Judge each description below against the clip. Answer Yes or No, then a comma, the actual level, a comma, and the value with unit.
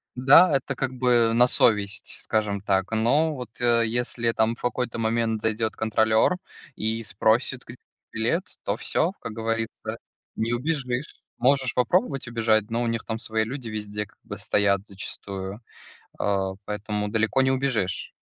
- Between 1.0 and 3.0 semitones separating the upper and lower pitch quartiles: Yes, narrow, 2.4 semitones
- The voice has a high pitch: No, low, 115 Hz